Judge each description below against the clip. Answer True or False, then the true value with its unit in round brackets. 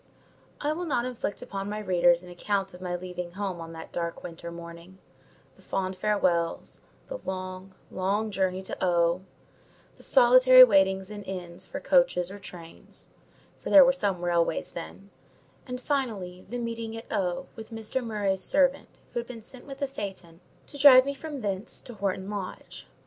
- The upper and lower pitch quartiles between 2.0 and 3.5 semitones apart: False (5.1 semitones)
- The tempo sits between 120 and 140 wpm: False (170 wpm)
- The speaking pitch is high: True (195 Hz)